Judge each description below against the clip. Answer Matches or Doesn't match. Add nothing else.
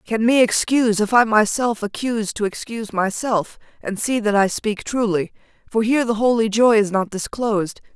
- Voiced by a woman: Matches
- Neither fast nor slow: Matches